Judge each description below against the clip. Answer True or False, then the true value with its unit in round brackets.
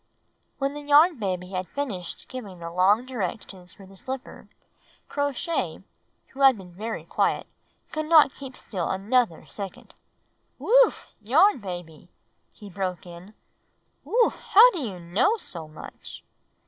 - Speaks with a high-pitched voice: True (210 Hz)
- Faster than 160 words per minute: False (145 wpm)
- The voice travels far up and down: True (7.6 semitones)